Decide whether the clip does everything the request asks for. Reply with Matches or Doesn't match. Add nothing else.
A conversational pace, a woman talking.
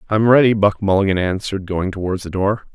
Doesn't match